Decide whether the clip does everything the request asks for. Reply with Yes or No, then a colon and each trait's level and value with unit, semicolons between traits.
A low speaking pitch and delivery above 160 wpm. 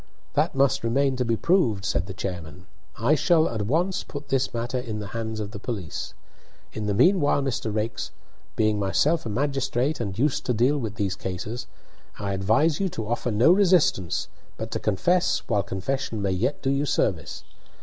Yes: low, 115 Hz; average, 185 wpm